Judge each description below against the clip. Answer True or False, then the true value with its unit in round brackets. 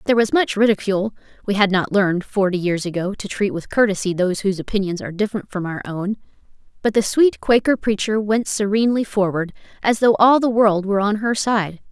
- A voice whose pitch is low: False (205 Hz)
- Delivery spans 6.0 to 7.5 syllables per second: True (6.1 syllables/s)